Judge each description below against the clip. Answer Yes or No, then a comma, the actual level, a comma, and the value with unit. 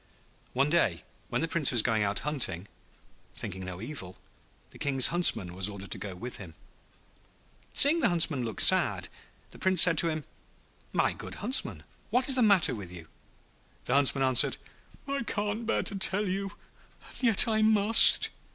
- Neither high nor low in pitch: Yes, medium, 150 Hz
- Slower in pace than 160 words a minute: No, average, 170 wpm